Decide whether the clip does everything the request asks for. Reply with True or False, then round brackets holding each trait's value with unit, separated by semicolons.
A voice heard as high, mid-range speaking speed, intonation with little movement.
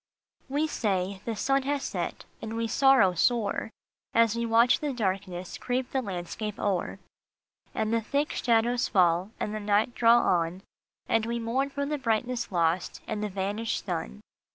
False (225 Hz; 175 wpm; 4.0 semitones)